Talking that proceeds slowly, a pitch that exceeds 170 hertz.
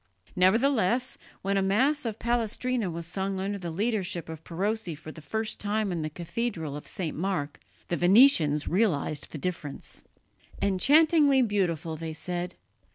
No: average, 150 wpm; high, 190 Hz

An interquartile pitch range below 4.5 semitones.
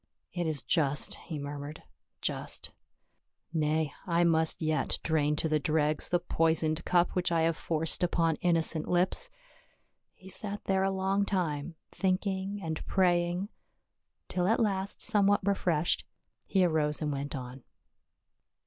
Yes: average, 3.5 semitones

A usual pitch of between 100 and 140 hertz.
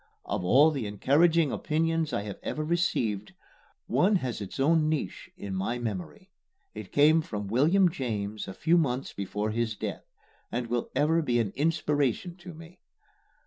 Yes: low, 135 Hz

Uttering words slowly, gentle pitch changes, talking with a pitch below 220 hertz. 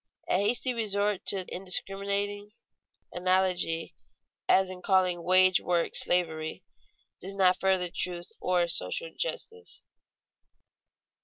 Yes: slow, 100 wpm; narrow, 2.0 semitones; medium, 185 Hz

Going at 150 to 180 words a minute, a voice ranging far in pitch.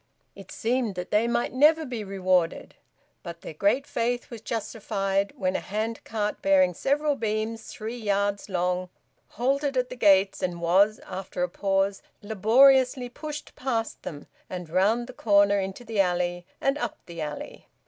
No: average, 160 wpm; average, 4.4 semitones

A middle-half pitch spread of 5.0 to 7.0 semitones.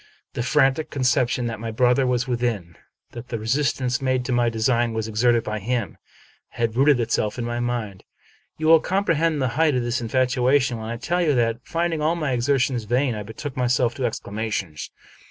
No: average, 2.7 semitones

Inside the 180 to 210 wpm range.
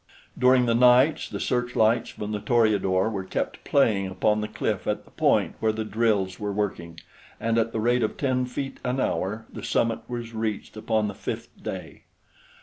Yes: average, 185 wpm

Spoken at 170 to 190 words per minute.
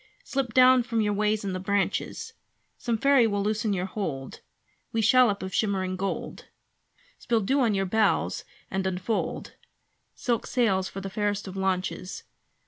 No: average, 155 wpm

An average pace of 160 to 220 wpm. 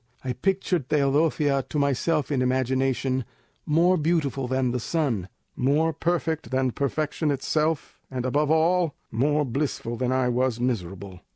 No: slow, 135 wpm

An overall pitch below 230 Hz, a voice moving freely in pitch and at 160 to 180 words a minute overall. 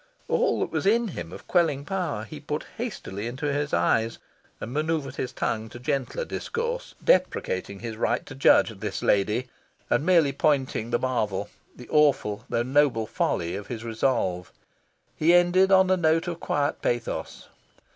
Yes: medium, 140 Hz; wide, 7.0 semitones; average, 165 wpm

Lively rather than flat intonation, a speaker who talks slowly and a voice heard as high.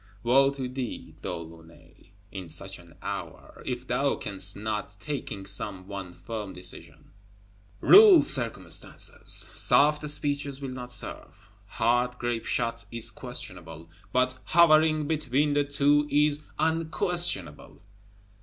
No: wide, 7.0 semitones; slow, 120 wpm; low, 125 Hz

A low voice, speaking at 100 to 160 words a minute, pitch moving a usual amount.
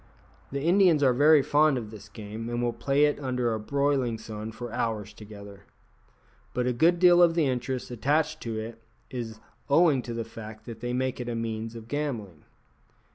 No: low, 120 Hz; average, 195 wpm; average, 4.3 semitones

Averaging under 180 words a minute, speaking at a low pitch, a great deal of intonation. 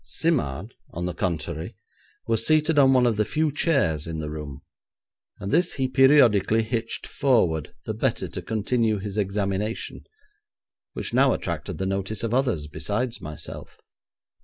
Yes: average, 150 wpm; low, 110 Hz; wide, 6.3 semitones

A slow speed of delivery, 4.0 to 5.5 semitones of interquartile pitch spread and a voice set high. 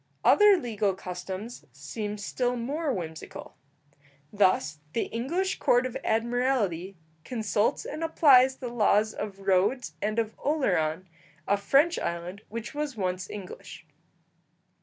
Yes: slow, 120 wpm; average, 5.2 semitones; high, 215 Hz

